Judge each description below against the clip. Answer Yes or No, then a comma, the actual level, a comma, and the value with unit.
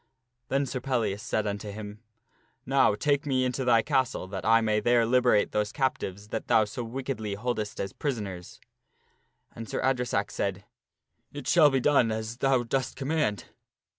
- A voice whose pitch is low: Yes, low, 115 Hz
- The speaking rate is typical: Yes, average, 180 wpm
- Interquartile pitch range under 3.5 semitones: No, average, 4.0 semitones